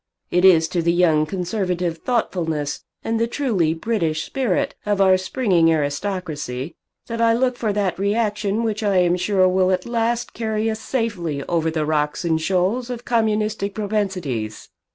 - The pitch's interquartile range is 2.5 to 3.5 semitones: No, average, 5.0 semitones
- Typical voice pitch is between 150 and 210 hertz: Yes, high, 190 Hz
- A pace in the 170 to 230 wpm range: No, average, 160 wpm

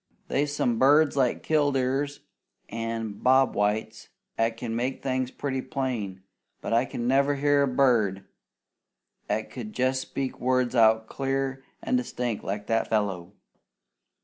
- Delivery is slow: Yes, slow, 130 wpm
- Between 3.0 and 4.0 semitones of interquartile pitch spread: Yes, average, 3.3 semitones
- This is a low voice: Yes, low, 125 Hz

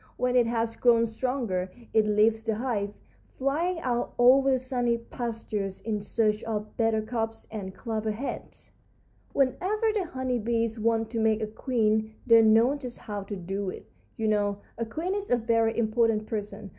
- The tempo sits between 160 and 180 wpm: Yes, average, 170 wpm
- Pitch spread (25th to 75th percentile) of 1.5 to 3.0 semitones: Yes, narrow, 2.5 semitones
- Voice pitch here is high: Yes, high, 225 Hz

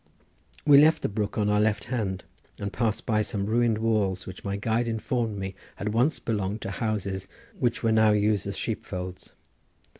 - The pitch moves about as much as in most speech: No, narrow, 2.3 semitones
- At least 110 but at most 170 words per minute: No, average, 185 wpm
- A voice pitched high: No, low, 105 Hz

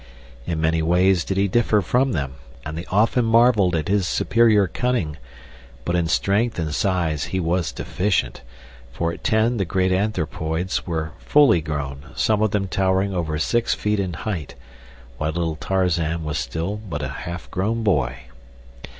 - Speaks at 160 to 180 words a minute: Yes, average, 165 wpm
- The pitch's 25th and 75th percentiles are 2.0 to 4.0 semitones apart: No, average, 4.5 semitones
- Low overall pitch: Yes, very low, 90 Hz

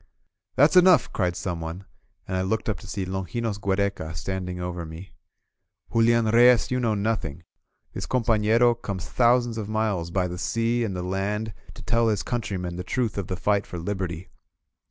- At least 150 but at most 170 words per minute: No, average, 195 wpm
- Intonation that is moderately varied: Yes, average, 4.1 semitones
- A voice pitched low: Yes, low, 100 Hz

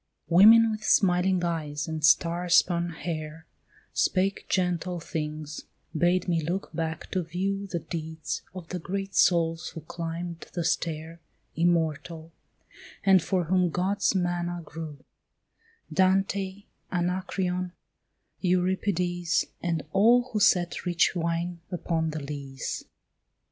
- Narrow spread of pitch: Yes, narrow, 2.2 semitones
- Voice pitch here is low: No, medium, 175 Hz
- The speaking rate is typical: No, slow, 115 wpm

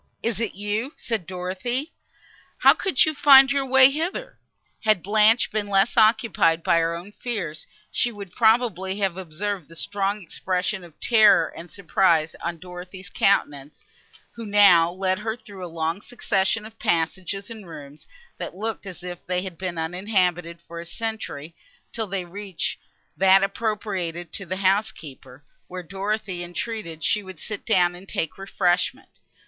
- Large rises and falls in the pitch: No, average, 3.8 semitones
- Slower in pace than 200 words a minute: Yes, average, 155 wpm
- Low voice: No, high, 190 Hz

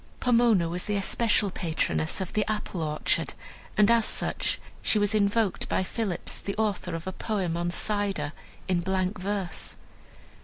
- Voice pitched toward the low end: No, high, 195 Hz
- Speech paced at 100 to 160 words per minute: Yes, average, 155 wpm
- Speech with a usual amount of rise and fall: Yes, average, 3.4 semitones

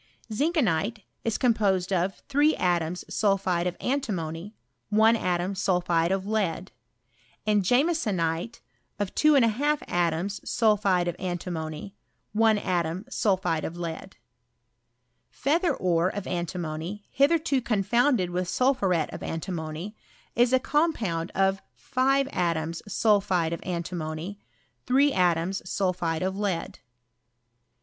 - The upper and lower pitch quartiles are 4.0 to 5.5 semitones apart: Yes, average, 4.7 semitones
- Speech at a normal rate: No, slow, 110 wpm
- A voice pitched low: No, high, 190 Hz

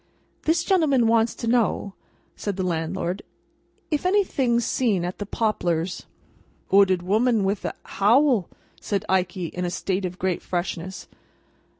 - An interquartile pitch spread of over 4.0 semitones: Yes, average, 4.6 semitones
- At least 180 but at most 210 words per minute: No, slow, 135 wpm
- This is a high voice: Yes, high, 200 Hz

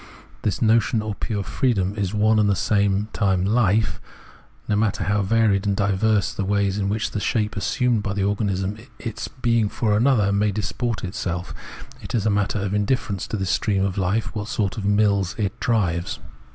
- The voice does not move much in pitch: Yes, narrow, 2.0 semitones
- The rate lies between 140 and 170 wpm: No, average, 190 wpm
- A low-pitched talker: Yes, low, 105 Hz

